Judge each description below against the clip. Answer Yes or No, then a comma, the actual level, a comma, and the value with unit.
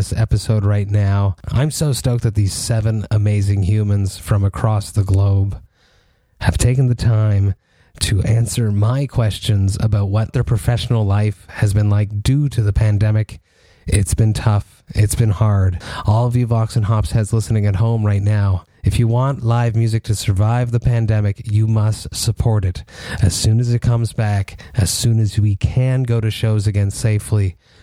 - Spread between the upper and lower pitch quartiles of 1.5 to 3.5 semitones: Yes, narrow, 2.4 semitones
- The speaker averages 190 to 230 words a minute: No, average, 175 wpm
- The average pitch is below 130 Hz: Yes, low, 105 Hz